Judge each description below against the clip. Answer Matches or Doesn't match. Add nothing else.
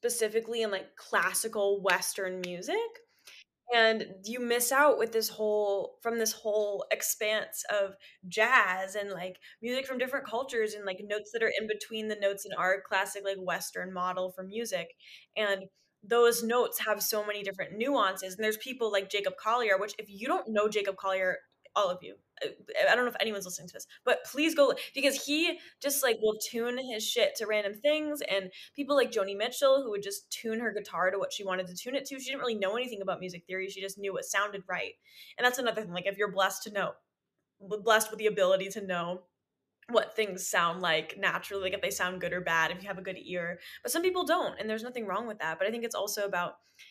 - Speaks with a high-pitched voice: Matches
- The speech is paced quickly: Matches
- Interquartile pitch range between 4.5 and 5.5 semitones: Doesn't match